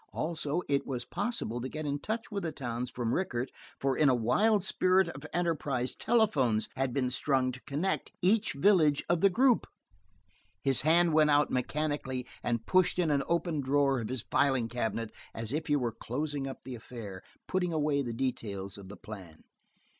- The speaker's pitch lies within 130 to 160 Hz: Yes, medium, 140 Hz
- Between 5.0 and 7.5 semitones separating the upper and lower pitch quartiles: Yes, average, 5.3 semitones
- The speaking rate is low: No, average, 185 wpm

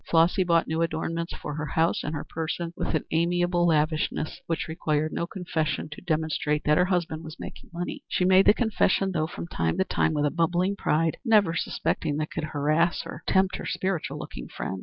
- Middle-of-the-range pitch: Yes, medium, 165 Hz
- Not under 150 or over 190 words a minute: No, fast, 205 wpm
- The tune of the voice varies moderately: No, narrow, 2.3 semitones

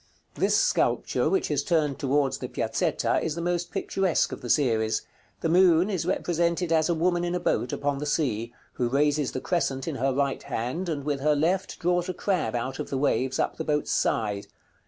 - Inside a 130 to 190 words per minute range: No, fast, 205 wpm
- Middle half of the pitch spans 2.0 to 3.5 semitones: No, average, 4.5 semitones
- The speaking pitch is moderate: Yes, medium, 150 Hz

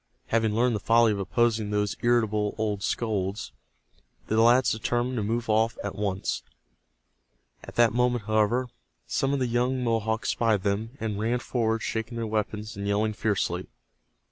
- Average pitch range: No, narrow, 2.1 semitones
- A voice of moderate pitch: No, low, 110 Hz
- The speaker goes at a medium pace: Yes, average, 160 wpm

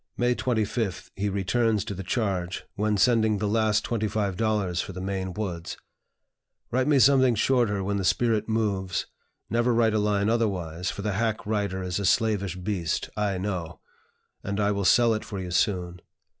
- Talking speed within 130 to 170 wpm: No, average, 180 wpm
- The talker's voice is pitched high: No, low, 105 Hz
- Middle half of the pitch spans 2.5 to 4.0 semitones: Yes, average, 2.9 semitones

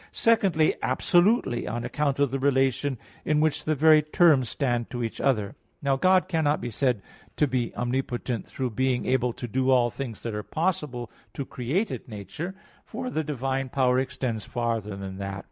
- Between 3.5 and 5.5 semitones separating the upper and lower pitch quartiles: Yes, average, 4.1 semitones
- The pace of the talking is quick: No, average, 175 wpm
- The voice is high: No, low, 130 Hz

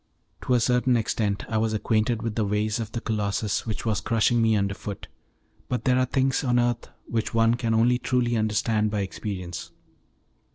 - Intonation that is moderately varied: No, narrow, 2.3 semitones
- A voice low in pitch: Yes, low, 115 Hz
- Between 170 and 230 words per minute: Yes, average, 190 wpm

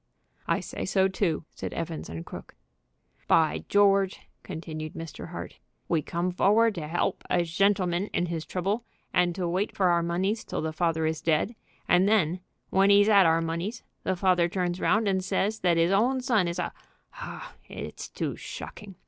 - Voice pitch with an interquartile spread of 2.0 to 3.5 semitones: Yes, average, 3.0 semitones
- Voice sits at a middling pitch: Yes, medium, 180 Hz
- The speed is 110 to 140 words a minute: No, average, 180 wpm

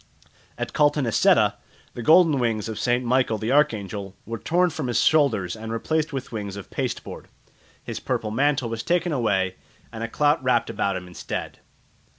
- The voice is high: No, low, 120 Hz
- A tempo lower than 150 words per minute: No, average, 165 wpm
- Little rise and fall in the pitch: No, wide, 5.4 semitones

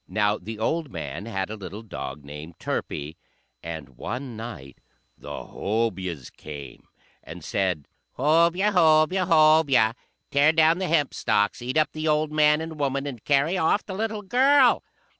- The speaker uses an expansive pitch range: Yes, wide, 8.6 semitones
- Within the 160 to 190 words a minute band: No, average, 150 wpm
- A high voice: No, medium, 140 Hz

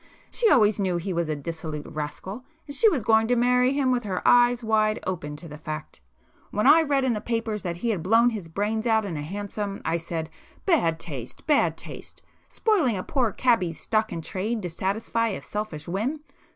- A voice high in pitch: Yes, high, 210 Hz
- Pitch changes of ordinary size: No, wide, 6.0 semitones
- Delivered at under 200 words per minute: No, fast, 205 wpm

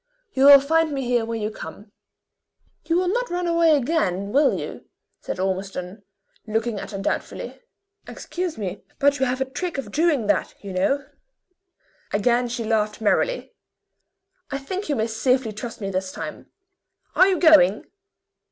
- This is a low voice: No, high, 245 Hz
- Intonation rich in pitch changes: Yes, wide, 6.7 semitones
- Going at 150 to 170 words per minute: Yes, average, 160 wpm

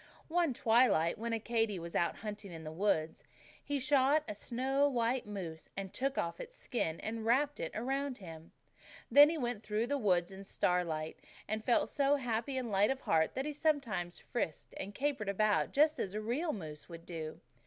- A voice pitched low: No, high, 225 Hz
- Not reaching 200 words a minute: No, fast, 205 wpm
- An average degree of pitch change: No, wide, 7.0 semitones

